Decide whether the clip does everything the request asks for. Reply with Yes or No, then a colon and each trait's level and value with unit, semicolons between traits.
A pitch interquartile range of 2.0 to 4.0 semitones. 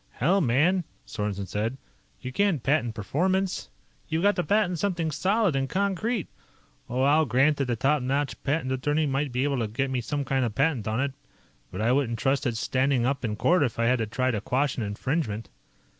No: average, 4.8 semitones